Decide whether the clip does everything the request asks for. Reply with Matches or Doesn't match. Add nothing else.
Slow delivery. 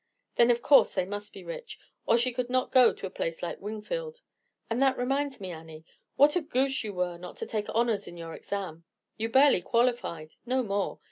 Doesn't match